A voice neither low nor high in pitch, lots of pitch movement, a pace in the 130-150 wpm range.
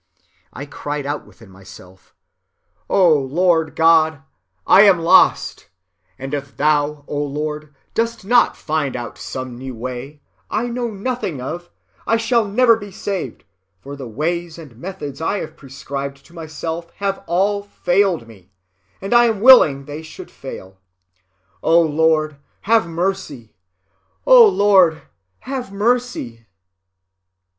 Yes: medium, 160 Hz; wide, 6.2 semitones; slow, 135 wpm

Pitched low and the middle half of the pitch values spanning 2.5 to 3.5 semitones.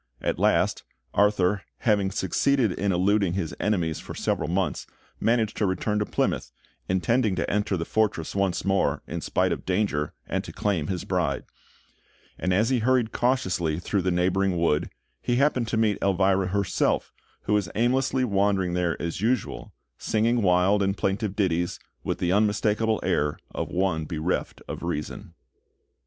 Yes: low, 100 Hz; average, 3.2 semitones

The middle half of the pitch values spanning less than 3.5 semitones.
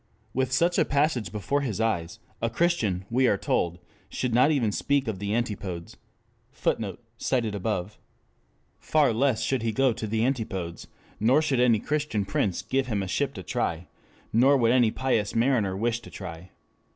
No: average, 4.6 semitones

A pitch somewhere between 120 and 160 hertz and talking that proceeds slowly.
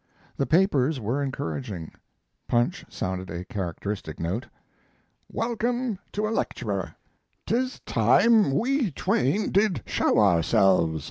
Yes: low, 135 Hz; slow, 110 wpm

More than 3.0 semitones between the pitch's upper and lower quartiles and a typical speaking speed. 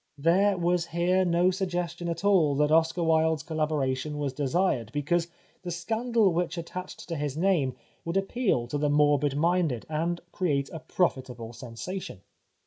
Yes: average, 3.5 semitones; average, 160 wpm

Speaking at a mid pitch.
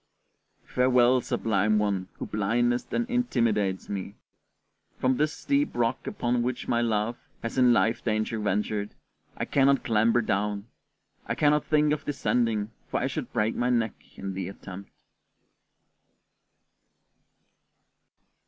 No: low, 115 Hz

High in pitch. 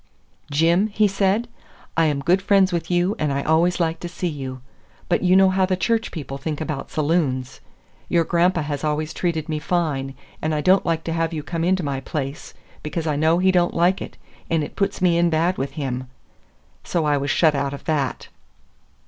No: medium, 165 Hz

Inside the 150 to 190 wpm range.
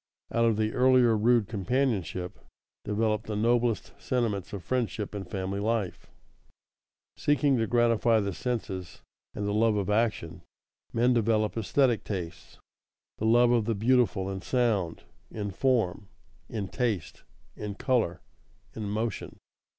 No: slow, 135 wpm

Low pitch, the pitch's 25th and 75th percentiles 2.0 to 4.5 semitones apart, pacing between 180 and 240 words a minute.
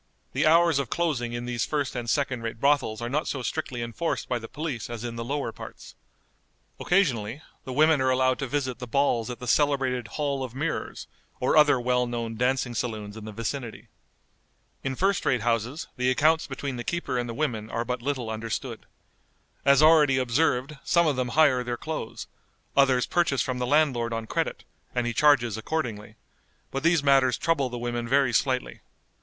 Yes: low, 130 Hz; average, 3.4 semitones; average, 190 wpm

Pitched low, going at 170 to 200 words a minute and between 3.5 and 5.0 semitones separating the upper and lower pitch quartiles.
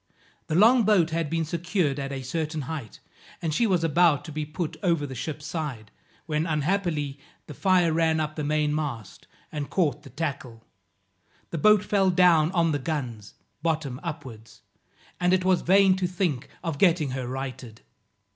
No: medium, 155 Hz; average, 175 wpm; average, 3.8 semitones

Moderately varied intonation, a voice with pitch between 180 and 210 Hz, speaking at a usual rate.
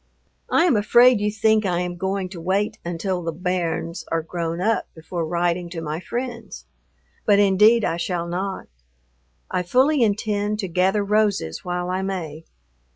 Yes: average, 3.4 semitones; medium, 185 Hz; average, 160 wpm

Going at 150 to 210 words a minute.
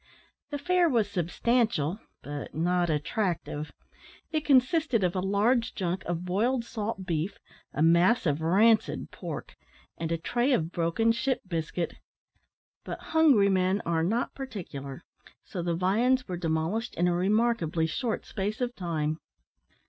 No: average, 140 wpm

